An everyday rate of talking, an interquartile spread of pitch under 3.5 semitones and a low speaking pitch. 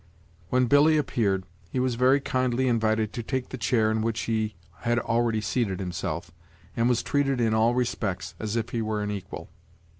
Yes: average, 185 wpm; narrow, 2.6 semitones; low, 115 Hz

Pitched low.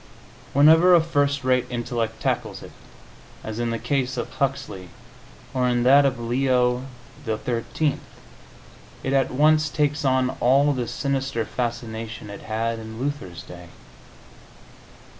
Yes: low, 125 Hz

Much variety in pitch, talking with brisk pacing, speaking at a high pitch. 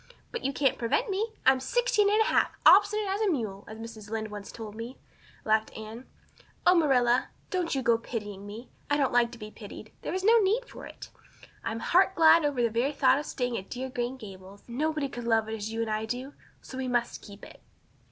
Yes: wide, 6.0 semitones; fast, 230 wpm; high, 245 Hz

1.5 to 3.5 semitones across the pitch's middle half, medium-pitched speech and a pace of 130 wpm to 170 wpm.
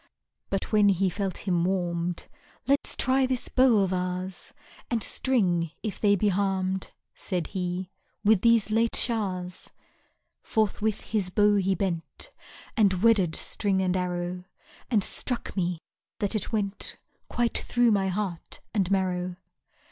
No: average, 3.0 semitones; high, 195 Hz; average, 140 wpm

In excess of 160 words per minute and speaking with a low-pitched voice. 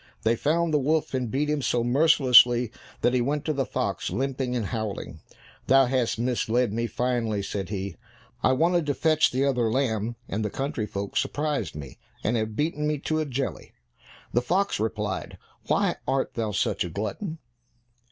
Yes: average, 180 wpm; low, 125 Hz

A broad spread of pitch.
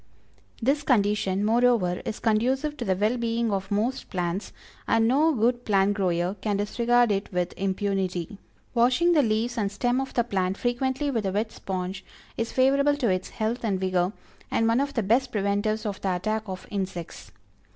No: average, 4.0 semitones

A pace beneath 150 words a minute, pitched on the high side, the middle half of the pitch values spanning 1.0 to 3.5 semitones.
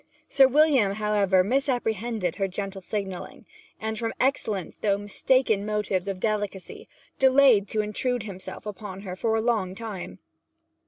Yes: average, 140 wpm; high, 210 Hz; average, 3.0 semitones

